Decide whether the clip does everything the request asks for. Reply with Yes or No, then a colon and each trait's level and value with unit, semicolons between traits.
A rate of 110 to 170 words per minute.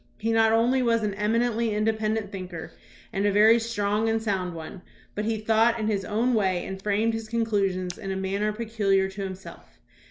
No: average, 200 wpm